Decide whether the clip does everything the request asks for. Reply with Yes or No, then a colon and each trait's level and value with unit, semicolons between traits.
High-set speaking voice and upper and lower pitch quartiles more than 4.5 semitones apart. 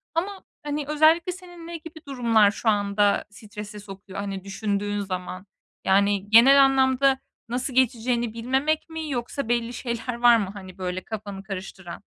Yes: high, 230 Hz; average, 5.2 semitones